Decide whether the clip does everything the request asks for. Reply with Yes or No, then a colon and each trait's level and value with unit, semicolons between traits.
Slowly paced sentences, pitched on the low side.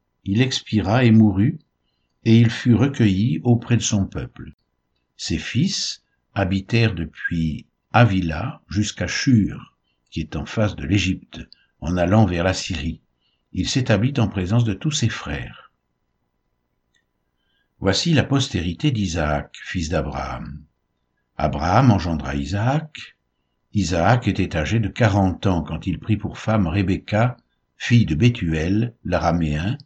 Yes: slow, 125 wpm; low, 100 Hz